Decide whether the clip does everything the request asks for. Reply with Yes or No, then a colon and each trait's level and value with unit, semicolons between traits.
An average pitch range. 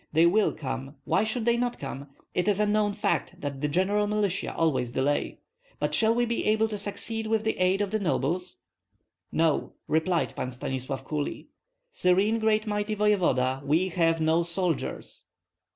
No: wide, 5.8 semitones